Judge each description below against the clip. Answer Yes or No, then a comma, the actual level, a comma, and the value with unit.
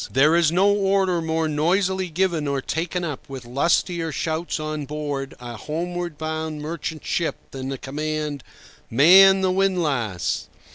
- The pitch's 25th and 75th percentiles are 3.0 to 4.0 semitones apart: Yes, average, 3.4 semitones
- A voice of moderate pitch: Yes, medium, 160 Hz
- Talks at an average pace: Yes, average, 145 wpm